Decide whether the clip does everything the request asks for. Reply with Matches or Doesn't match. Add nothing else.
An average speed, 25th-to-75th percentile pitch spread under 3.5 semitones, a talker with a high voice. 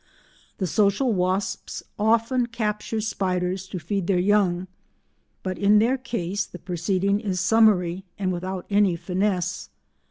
Doesn't match